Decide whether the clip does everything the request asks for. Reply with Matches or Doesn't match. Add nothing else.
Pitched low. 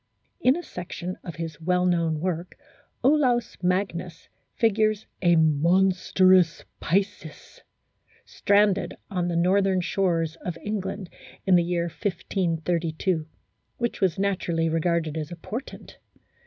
Doesn't match